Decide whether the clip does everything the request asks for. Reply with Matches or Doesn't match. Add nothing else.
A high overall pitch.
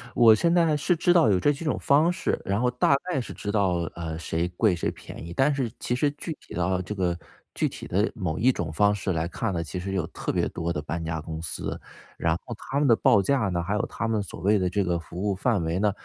Doesn't match